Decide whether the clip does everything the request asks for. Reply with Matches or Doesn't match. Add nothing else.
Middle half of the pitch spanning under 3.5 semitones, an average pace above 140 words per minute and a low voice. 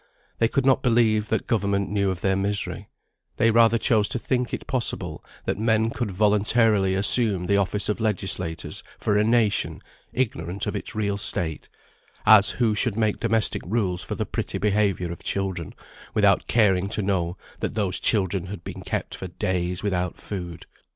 Matches